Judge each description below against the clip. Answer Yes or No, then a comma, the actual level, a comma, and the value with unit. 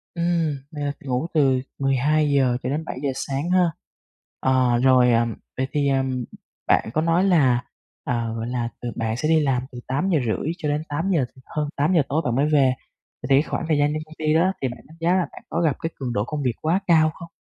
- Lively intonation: No, average, 3.8 semitones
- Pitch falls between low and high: Yes, medium, 145 Hz